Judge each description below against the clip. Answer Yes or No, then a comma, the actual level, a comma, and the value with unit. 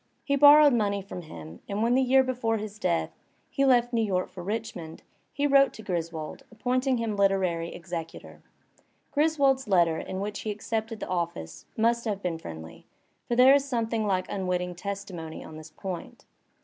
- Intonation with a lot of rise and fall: Yes, wide, 5.7 semitones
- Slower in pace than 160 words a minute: No, average, 175 wpm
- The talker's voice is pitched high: Yes, high, 205 Hz